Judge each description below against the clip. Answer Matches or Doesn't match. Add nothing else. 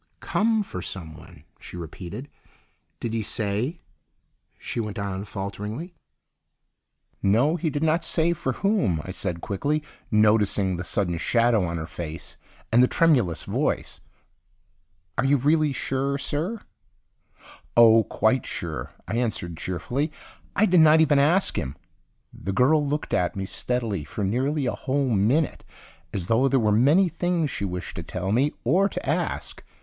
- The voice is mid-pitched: Doesn't match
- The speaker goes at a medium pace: Matches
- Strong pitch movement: Matches